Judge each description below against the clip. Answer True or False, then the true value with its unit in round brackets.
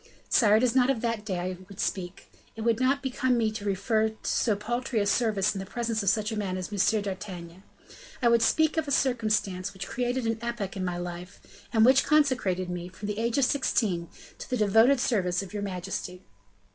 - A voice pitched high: True (215 Hz)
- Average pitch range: True (4.1 semitones)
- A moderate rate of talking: False (220 wpm)